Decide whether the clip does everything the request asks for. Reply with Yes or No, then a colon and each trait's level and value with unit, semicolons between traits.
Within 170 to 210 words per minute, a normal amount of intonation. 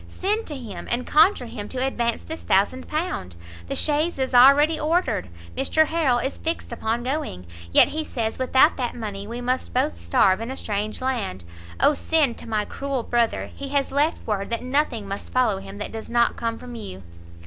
Yes: average, 195 wpm; average, 4.6 semitones